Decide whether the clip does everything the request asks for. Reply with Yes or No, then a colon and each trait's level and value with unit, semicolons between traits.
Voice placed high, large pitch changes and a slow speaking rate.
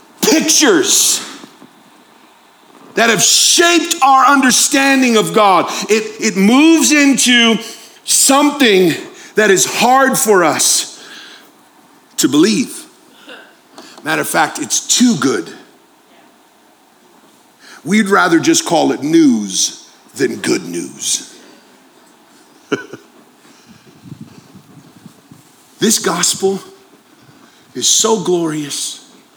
Yes: very high, 280 Hz; wide, 6.9 semitones; slow, 80 wpm